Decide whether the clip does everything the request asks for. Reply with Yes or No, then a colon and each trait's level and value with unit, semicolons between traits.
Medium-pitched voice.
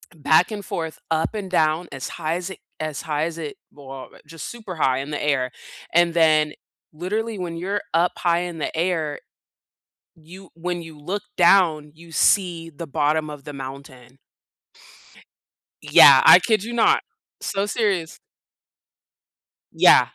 Yes: medium, 165 Hz